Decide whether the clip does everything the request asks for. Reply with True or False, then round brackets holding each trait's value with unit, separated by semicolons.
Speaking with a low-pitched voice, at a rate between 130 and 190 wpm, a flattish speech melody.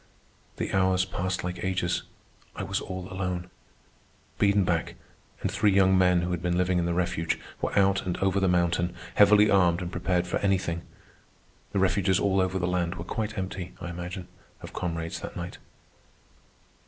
True (90 Hz; 170 wpm; 1.5 semitones)